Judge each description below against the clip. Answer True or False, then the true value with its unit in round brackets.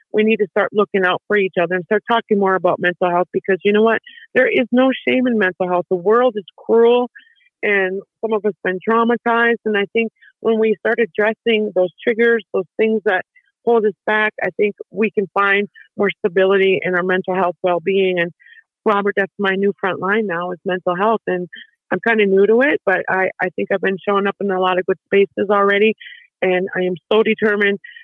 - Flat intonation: False (3.1 semitones)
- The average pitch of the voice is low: False (205 Hz)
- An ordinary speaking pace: False (220 wpm)